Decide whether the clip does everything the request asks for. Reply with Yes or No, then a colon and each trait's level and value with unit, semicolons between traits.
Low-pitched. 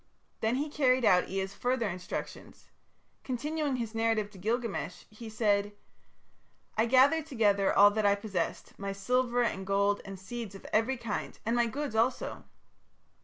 No: high, 220 Hz